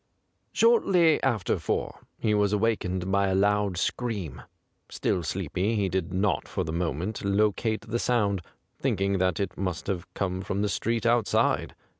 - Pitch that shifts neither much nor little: Yes, average, 3.0 semitones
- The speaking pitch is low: Yes, low, 100 Hz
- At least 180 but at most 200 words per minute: No, average, 160 wpm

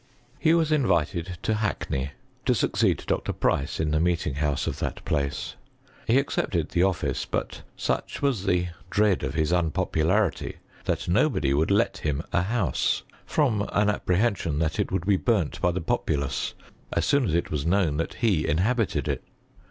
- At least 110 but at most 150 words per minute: No, average, 175 wpm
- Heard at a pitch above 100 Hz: No, very low, 90 Hz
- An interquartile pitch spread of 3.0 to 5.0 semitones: No, wide, 5.4 semitones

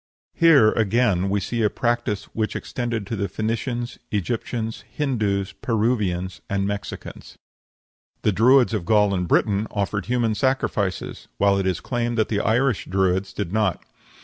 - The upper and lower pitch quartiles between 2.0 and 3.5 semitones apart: Yes, average, 3.2 semitones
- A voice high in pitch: No, low, 105 Hz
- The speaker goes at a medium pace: Yes, average, 150 wpm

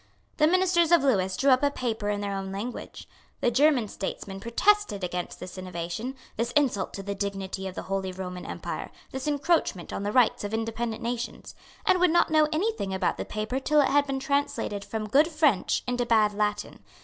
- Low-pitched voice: No, high, 230 Hz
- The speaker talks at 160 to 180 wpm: No, average, 200 wpm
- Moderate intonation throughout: No, wide, 6.5 semitones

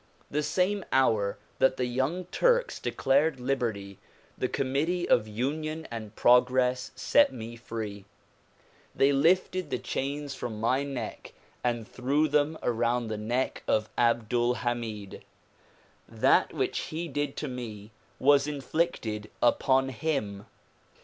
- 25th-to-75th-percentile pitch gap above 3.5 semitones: Yes, average, 4.1 semitones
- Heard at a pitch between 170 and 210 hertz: No, low, 130 Hz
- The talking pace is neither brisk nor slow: No, slow, 125 wpm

